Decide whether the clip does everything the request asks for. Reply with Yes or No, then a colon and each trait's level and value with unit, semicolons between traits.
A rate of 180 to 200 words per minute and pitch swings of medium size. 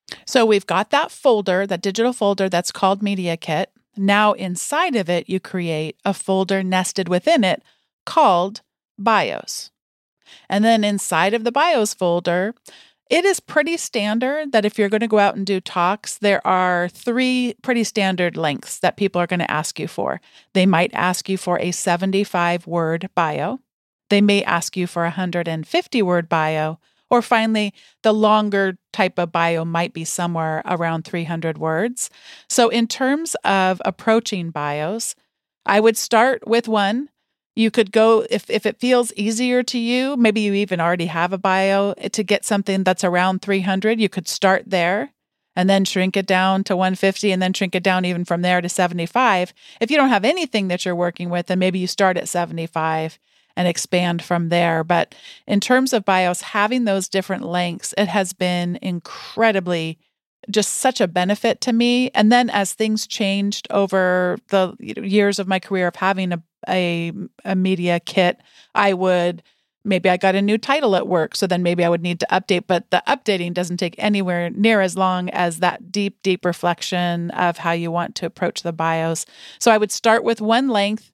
Yes: average, 190 wpm; average, 3.4 semitones